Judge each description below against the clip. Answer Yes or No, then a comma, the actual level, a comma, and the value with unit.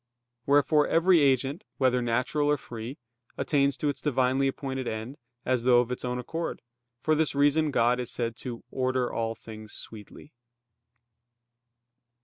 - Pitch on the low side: Yes, low, 130 Hz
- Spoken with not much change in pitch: No, average, 3.1 semitones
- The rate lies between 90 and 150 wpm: Yes, average, 145 wpm